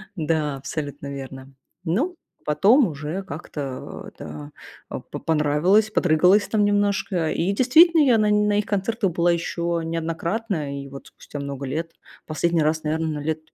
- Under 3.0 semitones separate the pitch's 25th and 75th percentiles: No, wide, 5.5 semitones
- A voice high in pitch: No, medium, 165 Hz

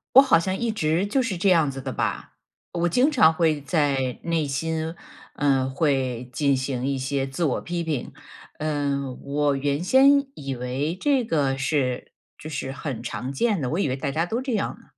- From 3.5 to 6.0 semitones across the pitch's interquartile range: Yes, average, 4.3 semitones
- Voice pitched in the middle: Yes, medium, 150 Hz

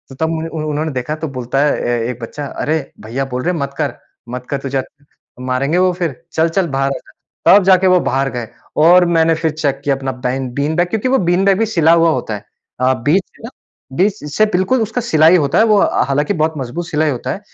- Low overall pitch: No, medium, 155 Hz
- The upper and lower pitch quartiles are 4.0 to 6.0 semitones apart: Yes, average, 4.6 semitones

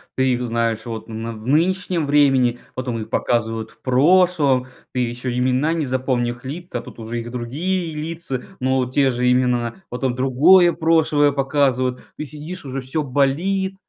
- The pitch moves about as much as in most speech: Yes, average, 3.8 semitones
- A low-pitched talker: Yes, low, 130 Hz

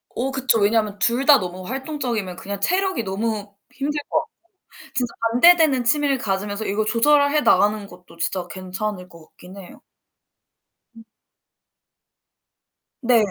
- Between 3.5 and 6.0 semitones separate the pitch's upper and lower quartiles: Yes, wide, 5.5 semitones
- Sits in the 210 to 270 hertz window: Yes, high, 225 Hz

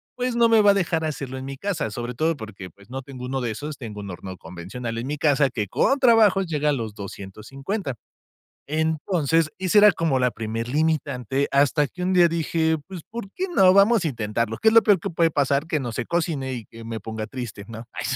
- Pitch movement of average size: No, wide, 6.5 semitones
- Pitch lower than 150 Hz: Yes, medium, 140 Hz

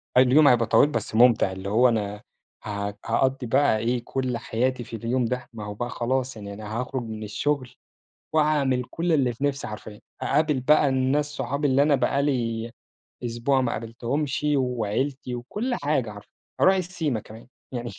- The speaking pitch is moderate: No, low, 125 Hz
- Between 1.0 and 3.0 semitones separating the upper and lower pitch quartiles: No, average, 3.7 semitones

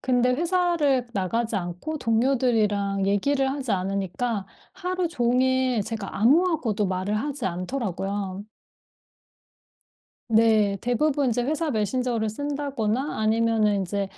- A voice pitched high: Yes, high, 230 Hz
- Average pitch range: Yes, average, 5.0 semitones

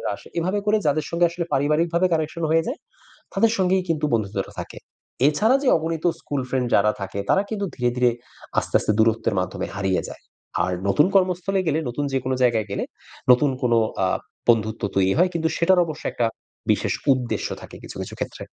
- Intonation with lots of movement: Yes, wide, 6.8 semitones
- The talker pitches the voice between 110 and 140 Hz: No, medium, 150 Hz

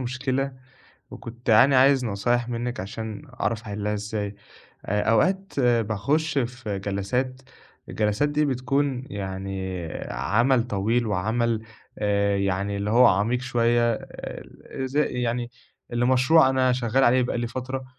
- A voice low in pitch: Yes, low, 120 Hz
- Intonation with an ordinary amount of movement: Yes, average, 3.8 semitones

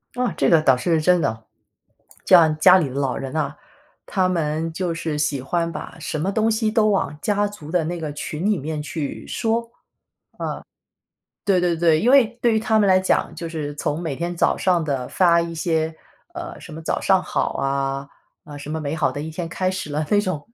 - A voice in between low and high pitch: Yes, medium, 165 Hz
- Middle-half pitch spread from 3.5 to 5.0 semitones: Yes, average, 3.8 semitones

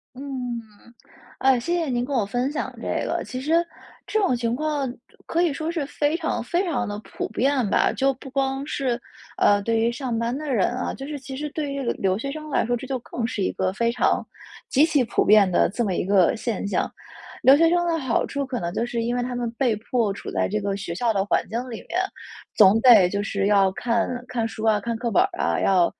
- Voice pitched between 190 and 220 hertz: No, high, 245 Hz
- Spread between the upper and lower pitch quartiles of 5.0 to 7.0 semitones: No, average, 4.5 semitones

